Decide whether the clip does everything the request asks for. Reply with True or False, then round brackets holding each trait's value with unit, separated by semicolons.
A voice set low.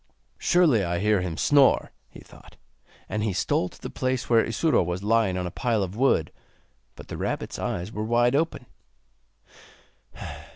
True (110 Hz)